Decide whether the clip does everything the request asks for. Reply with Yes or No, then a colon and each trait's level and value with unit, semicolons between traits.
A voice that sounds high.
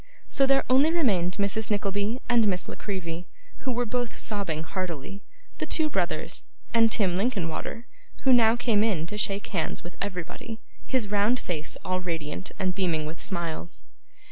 Yes: high, 200 Hz